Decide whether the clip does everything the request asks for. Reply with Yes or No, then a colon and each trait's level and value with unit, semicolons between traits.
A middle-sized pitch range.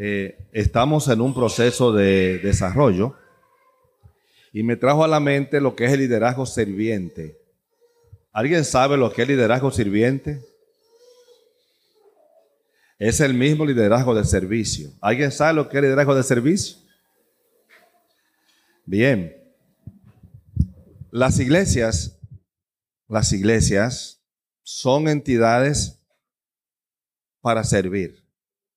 No: wide, 5.7 semitones